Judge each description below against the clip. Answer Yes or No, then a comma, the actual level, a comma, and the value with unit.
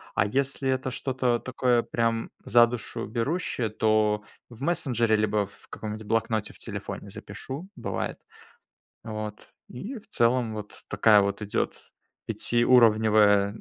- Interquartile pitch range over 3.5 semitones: No, average, 3.0 semitones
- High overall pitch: No, low, 115 Hz